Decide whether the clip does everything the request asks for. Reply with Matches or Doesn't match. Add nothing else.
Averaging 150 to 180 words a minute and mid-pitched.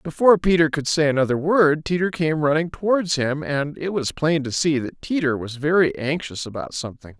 Doesn't match